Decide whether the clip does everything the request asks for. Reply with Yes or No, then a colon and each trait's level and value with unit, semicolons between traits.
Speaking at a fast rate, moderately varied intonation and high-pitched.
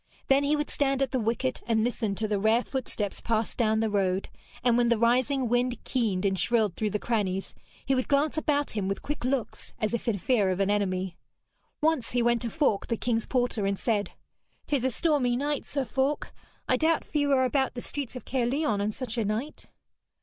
Yes: fast, 215 wpm; average, 4.1 semitones; high, 240 Hz